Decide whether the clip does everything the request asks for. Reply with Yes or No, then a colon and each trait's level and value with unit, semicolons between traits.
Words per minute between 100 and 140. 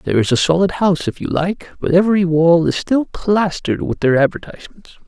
No: average, 200 wpm